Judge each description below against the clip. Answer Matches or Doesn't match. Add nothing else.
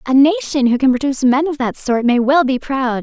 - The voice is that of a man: Doesn't match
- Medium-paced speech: Doesn't match